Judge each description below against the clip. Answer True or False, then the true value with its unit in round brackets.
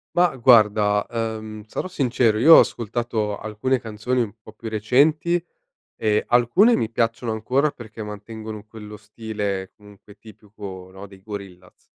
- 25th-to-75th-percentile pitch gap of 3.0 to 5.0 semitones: False (2.4 semitones)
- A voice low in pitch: True (110 Hz)